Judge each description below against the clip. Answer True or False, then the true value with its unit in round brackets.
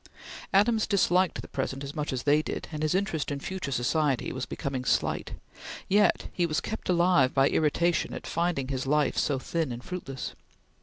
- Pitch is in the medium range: True (150 Hz)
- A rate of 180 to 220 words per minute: True (185 wpm)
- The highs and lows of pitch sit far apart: False (4.7 semitones)